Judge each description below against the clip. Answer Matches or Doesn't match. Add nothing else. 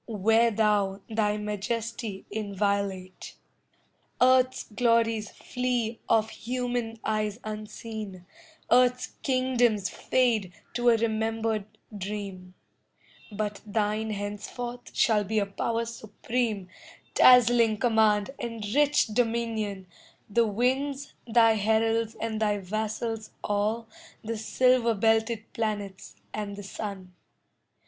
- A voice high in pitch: Matches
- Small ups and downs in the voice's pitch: Matches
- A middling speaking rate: Doesn't match